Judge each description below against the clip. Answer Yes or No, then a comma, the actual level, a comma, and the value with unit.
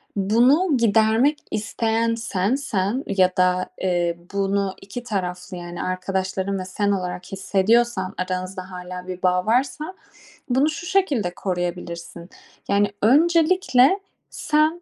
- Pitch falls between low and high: No, high, 200 Hz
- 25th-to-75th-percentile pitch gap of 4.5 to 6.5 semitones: Yes, average, 5.2 semitones